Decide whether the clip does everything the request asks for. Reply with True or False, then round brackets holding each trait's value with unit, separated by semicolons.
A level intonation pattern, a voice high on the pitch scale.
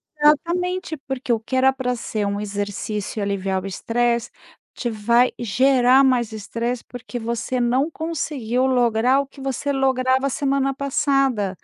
False (3.3 semitones; 250 Hz)